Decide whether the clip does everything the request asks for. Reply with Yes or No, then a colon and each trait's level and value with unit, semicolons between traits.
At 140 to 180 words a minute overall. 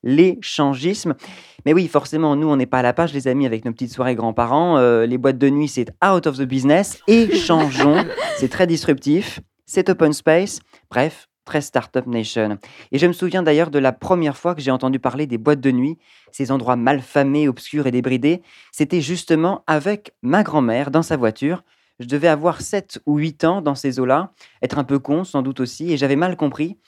No: average, 205 wpm